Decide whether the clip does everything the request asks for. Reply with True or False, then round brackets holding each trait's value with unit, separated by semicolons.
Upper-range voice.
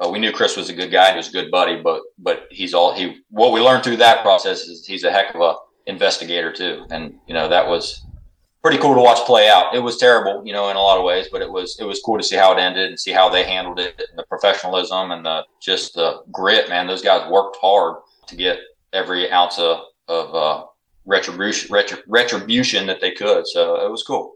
False (105 Hz)